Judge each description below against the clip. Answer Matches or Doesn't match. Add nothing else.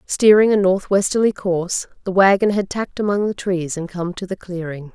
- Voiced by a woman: Matches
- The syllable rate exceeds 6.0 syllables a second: Doesn't match